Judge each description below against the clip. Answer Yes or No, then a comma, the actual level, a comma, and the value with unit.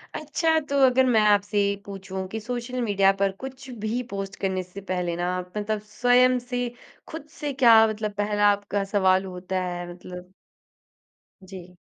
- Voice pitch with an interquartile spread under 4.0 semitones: No, average, 4.7 semitones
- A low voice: No, high, 205 Hz